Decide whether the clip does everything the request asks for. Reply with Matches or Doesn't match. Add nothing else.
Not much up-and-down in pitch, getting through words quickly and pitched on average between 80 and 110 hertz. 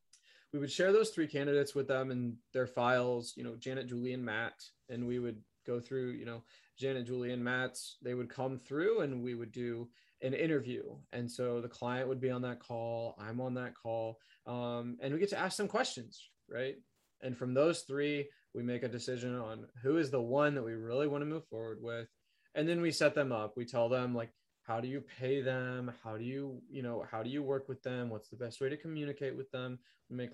Doesn't match